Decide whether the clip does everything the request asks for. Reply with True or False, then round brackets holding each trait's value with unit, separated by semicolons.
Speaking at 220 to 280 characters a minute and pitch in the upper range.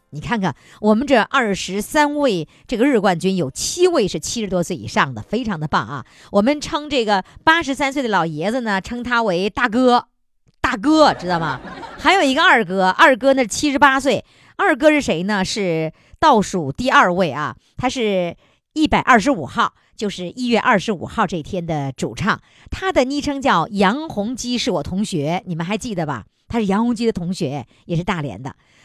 True (275 characters per minute; 210 Hz)